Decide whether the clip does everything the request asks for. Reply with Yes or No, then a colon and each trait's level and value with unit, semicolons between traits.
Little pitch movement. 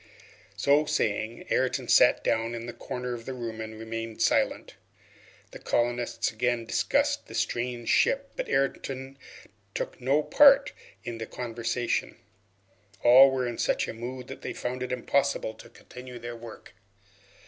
Yes: narrow, 2.1 semitones